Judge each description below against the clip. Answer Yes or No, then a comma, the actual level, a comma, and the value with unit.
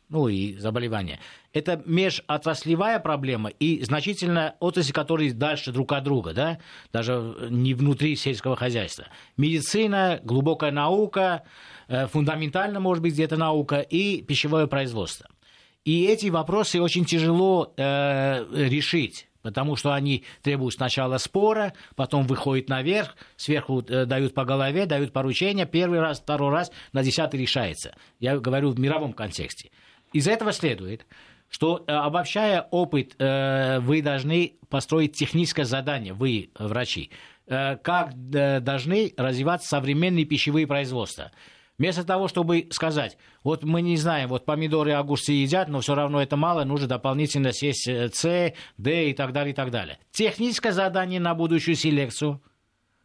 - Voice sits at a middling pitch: Yes, medium, 145 Hz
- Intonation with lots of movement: No, average, 4.1 semitones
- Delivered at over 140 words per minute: No, average, 135 wpm